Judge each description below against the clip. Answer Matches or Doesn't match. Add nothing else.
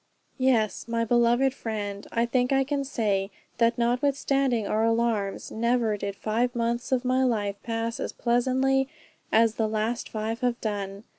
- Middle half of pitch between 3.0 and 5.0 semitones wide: Doesn't match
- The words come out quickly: Doesn't match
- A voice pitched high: Matches